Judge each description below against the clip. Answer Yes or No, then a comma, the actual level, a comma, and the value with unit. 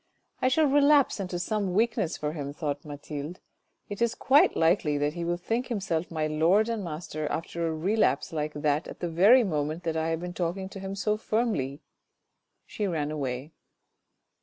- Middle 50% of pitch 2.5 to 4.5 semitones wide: No, wide, 5.4 semitones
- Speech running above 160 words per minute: Yes, average, 190 wpm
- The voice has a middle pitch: Yes, medium, 170 Hz